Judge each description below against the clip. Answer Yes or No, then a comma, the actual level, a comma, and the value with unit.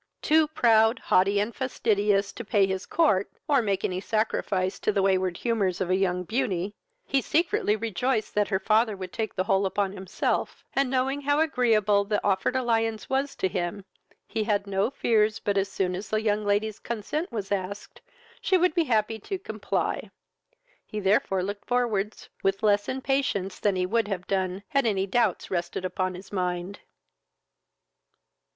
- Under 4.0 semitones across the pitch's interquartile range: Yes, average, 3.4 semitones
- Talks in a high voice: Yes, high, 205 Hz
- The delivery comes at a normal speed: Yes, average, 170 wpm